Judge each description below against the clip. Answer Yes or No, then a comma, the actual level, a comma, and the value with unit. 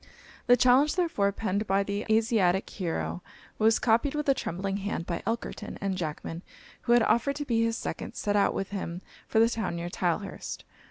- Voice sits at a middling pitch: No, high, 205 Hz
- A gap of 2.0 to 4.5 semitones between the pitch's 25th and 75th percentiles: Yes, average, 3.7 semitones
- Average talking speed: Yes, average, 185 wpm